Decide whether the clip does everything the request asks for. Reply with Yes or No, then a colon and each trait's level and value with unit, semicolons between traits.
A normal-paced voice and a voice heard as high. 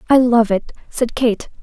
Yes: average, 185 wpm; high, 235 Hz